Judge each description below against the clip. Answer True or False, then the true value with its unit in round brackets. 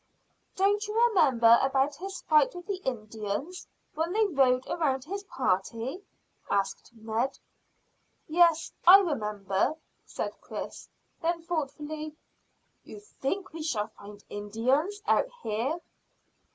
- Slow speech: True (115 wpm)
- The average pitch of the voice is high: True (295 Hz)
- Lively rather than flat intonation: True (7.6 semitones)